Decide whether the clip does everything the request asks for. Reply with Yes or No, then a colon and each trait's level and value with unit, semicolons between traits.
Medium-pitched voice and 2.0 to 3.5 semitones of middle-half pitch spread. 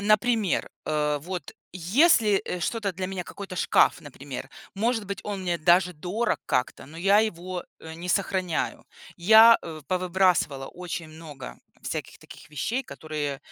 No: medium, 180 Hz; average, 4.1 semitones